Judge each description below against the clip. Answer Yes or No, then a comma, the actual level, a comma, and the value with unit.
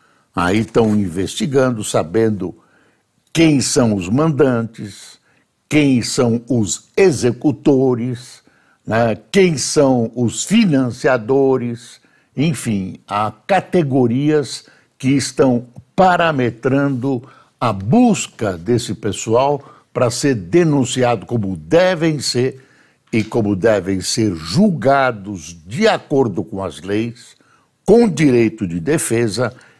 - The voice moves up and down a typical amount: Yes, average, 4.5 semitones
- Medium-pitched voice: No, low, 125 Hz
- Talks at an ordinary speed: No, slow, 95 wpm